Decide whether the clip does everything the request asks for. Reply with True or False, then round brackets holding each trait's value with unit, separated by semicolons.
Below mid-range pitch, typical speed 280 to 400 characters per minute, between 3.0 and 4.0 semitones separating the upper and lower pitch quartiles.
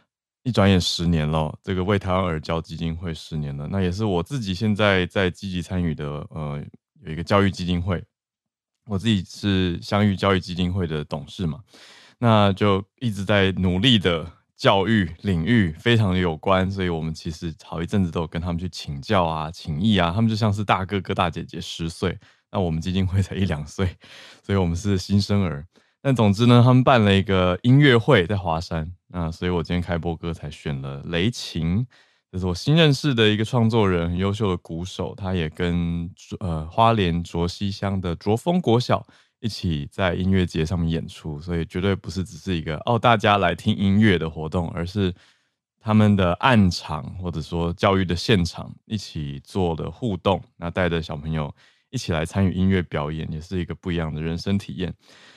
True (90 Hz; 290 characters per minute; 3.5 semitones)